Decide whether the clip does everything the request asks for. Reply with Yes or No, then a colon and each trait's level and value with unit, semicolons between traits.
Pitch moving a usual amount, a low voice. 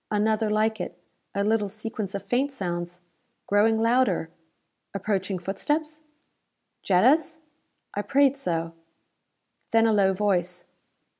No: average, 3.3 semitones; high, 210 Hz